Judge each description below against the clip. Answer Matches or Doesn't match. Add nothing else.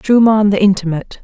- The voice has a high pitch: Matches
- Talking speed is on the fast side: Doesn't match